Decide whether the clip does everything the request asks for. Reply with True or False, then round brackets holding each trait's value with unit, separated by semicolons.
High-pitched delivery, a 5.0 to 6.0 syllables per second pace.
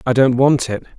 False (125 Hz; 5.2 syllables/s)